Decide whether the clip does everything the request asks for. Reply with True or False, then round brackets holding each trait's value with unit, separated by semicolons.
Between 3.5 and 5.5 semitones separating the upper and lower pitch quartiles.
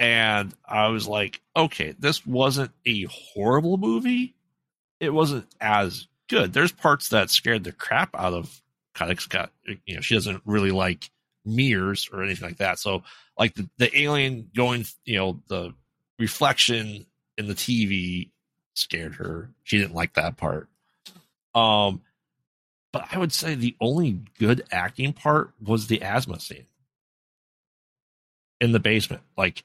True (4.9 semitones)